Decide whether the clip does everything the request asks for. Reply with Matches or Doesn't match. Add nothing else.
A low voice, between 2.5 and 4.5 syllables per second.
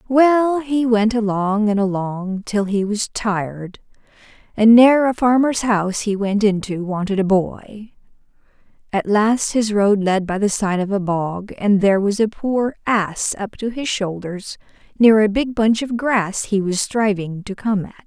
Doesn't match